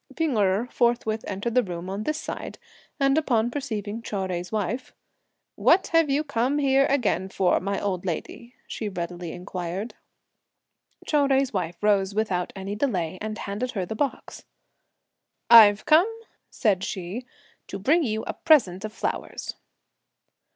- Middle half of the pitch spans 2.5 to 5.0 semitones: No, wide, 5.4 semitones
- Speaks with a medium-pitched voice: No, high, 215 Hz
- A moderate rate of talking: Yes, average, 150 wpm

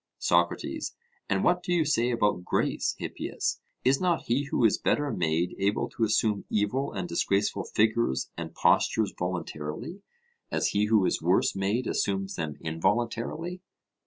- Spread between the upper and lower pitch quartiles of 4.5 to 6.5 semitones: Yes, wide, 5.4 semitones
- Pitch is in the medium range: No, low, 110 Hz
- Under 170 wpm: Yes, average, 150 wpm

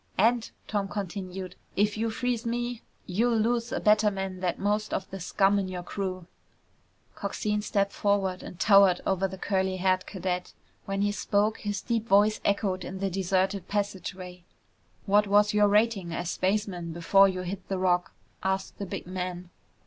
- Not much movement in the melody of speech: Yes, narrow, 2.1 semitones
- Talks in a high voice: Yes, high, 195 Hz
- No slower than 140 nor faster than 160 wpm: No, average, 170 wpm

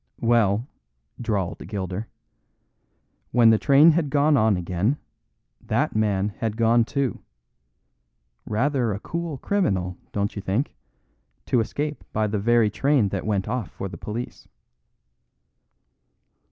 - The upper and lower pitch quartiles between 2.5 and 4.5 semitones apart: No, average, 4.9 semitones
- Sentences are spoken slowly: Yes, slow, 125 wpm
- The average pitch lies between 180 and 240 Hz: No, low, 110 Hz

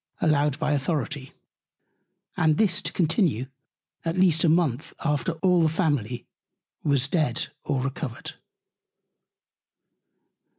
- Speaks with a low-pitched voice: No, medium, 150 Hz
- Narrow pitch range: No, average, 3.3 semitones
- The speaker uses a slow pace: Yes, slow, 110 wpm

